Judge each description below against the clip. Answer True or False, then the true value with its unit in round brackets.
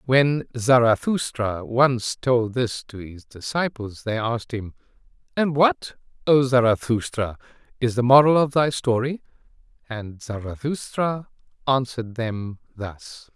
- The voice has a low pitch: True (125 Hz)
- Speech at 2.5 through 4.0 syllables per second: True (3.9 syllables/s)